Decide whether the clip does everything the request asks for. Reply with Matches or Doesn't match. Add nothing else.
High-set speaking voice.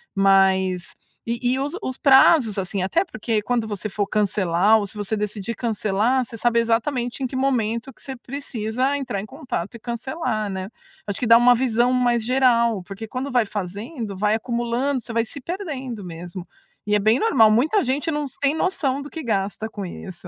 Matches